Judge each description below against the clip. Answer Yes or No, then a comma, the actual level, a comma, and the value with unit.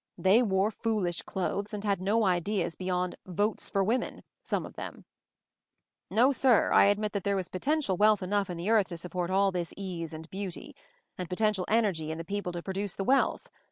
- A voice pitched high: Yes, high, 195 Hz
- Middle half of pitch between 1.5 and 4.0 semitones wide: Yes, average, 2.8 semitones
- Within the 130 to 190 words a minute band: No, fast, 205 wpm